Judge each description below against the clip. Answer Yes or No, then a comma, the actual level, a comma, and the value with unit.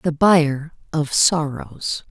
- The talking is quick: No, slow, 115 wpm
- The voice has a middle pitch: Yes, medium, 150 Hz